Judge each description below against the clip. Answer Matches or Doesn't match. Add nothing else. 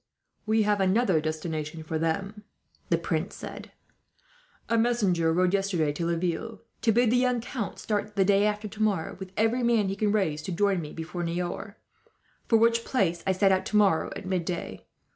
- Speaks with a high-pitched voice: Matches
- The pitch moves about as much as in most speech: Matches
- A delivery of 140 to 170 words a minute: Doesn't match